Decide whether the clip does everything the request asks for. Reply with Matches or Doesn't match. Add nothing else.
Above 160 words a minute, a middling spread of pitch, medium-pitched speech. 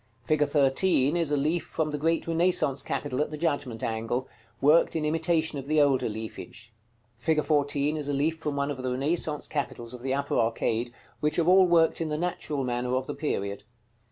Matches